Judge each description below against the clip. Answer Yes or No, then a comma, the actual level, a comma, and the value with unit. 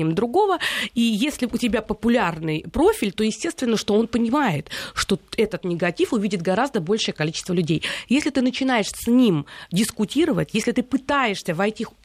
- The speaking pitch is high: Yes, high, 220 Hz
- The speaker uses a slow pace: No, average, 150 wpm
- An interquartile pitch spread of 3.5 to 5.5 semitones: Yes, average, 4.6 semitones